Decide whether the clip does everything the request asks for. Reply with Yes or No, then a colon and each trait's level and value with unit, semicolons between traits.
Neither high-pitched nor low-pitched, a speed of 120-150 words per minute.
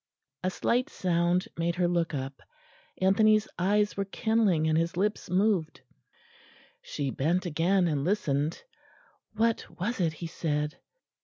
Yes: medium, 175 Hz; average, 140 wpm